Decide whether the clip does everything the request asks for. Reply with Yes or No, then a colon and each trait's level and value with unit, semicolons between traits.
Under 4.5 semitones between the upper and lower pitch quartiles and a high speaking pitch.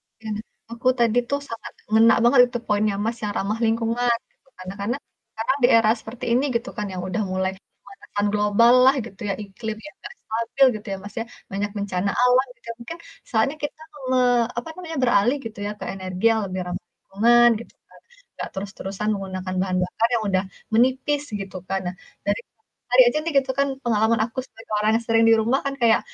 Yes: average, 3.2 semitones; high, 225 Hz